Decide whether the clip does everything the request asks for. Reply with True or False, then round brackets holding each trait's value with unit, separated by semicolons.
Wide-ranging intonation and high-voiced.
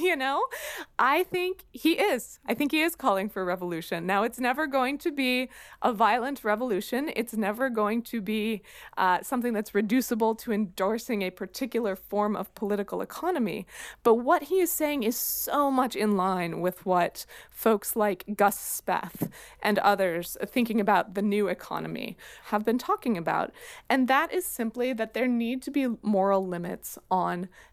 False (4.7 semitones; 225 Hz)